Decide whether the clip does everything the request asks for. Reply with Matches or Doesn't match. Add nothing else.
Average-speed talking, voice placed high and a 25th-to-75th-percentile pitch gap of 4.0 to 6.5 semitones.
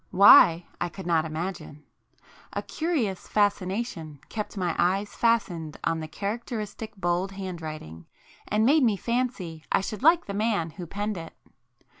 Matches